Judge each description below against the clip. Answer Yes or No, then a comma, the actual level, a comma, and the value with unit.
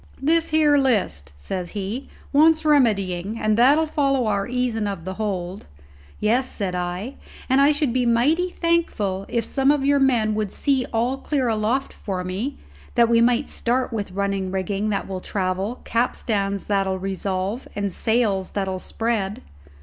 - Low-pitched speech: No, high, 220 Hz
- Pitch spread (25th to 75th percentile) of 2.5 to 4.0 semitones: No, average, 5.3 semitones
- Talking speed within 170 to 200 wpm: No, average, 160 wpm